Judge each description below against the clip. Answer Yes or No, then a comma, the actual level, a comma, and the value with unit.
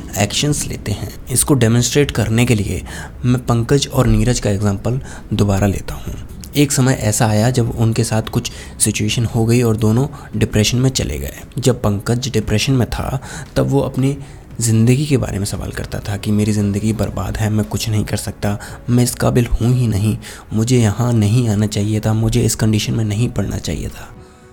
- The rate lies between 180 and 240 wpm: Yes, fast, 190 wpm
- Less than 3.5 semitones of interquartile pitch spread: Yes, average, 2.9 semitones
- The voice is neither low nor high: No, low, 110 Hz